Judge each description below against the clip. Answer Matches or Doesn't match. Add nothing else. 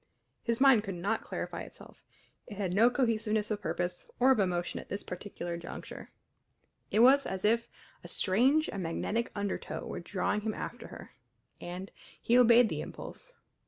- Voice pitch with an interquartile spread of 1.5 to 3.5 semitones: Doesn't match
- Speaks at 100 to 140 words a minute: Doesn't match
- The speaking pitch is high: Matches